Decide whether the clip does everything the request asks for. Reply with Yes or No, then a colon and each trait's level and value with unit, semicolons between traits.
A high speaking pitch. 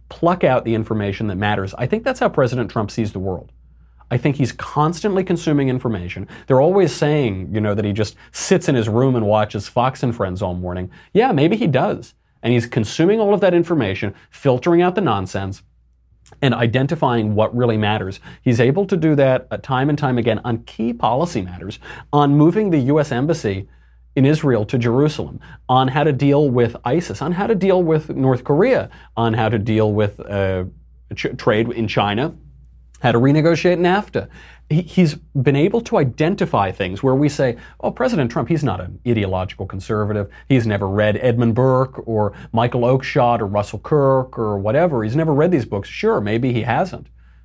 No: low, 120 Hz